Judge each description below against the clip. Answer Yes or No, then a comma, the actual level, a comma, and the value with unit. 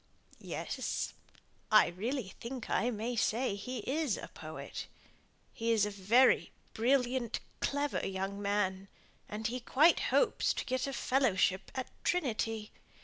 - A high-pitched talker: Yes, high, 235 Hz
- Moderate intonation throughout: Yes, average, 4.1 semitones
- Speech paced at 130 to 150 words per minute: Yes, slow, 135 wpm